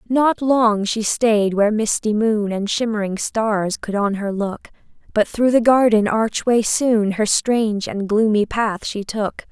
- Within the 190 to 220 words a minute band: No, average, 170 wpm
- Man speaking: No, female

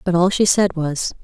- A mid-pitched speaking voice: Yes, medium, 175 Hz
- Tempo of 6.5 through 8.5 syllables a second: No, 4.8 syllables/s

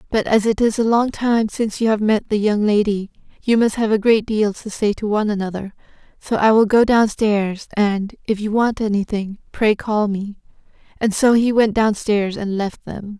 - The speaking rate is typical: No, fast, 210 wpm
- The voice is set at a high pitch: Yes, high, 215 Hz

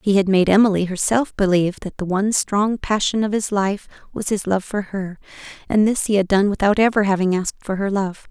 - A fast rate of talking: Yes, fast, 225 wpm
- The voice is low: No, high, 200 Hz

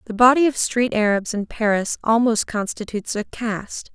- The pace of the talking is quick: No, average, 165 wpm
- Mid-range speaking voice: No, high, 220 Hz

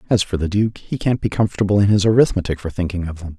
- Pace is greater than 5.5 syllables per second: Yes, 6.9 syllables/s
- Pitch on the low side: Yes, low, 100 Hz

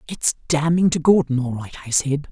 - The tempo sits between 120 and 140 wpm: No, fast, 205 wpm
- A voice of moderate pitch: Yes, medium, 150 Hz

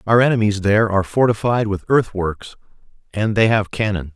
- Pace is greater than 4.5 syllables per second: Yes, 5.5 syllables/s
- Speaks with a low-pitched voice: Yes, low, 105 Hz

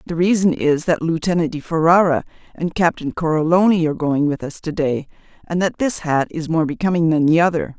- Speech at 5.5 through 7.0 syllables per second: Yes, 5.7 syllables/s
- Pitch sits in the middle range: Yes, medium, 165 Hz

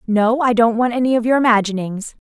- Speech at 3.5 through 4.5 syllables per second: No, 5.9 syllables/s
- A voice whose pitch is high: Yes, high, 230 Hz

